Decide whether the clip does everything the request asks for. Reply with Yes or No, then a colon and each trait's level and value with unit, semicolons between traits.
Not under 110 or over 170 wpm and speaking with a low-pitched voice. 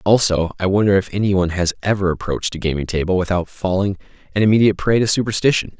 No: average, 195 wpm; very low, 95 Hz